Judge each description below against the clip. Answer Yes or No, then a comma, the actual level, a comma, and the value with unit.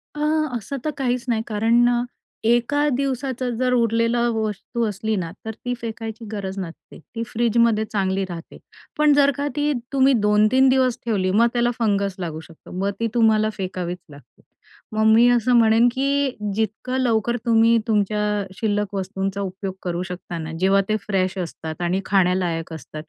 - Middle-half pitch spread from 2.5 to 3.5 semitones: No, average, 3.9 semitones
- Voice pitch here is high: Yes, high, 220 Hz